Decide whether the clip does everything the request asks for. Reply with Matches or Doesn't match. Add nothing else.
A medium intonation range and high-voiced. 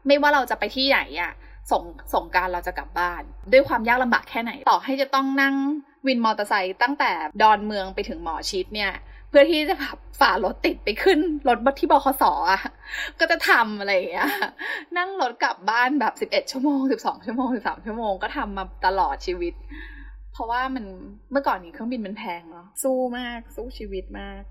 Doesn't match